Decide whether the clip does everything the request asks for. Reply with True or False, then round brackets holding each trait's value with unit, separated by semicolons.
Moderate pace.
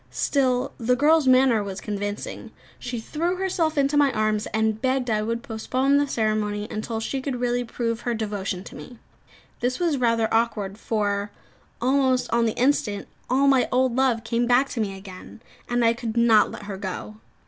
True (180 wpm)